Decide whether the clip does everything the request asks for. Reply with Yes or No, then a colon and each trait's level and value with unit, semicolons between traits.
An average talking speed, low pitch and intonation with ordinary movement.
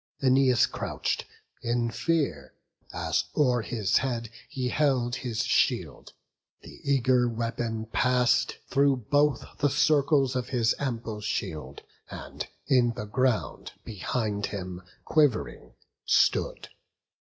No: slow, 110 wpm; low, 125 Hz; average, 3.2 semitones